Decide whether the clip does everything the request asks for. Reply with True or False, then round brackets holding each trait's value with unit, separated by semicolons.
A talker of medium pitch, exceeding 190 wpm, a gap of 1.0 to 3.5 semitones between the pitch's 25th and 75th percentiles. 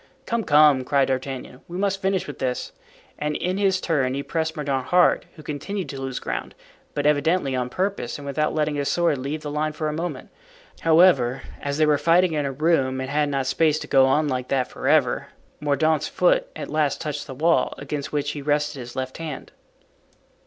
True (150 Hz; 200 wpm; 3.1 semitones)